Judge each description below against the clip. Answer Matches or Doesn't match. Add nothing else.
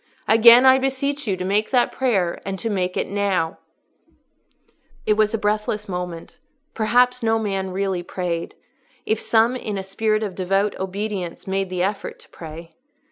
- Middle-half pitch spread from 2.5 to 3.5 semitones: Matches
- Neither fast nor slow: Matches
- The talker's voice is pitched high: Matches